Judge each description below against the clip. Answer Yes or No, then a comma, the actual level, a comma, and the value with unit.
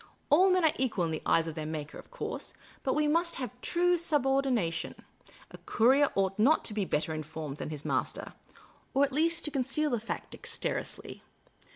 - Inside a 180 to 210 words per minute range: Yes, fast, 205 wpm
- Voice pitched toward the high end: Yes, very high, 260 Hz